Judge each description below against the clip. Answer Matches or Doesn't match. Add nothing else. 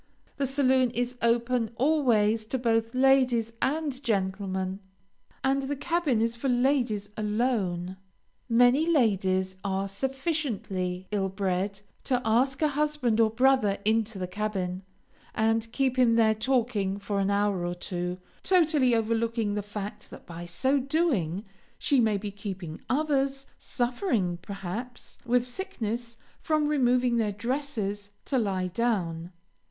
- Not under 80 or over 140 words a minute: Matches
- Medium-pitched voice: Doesn't match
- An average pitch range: Matches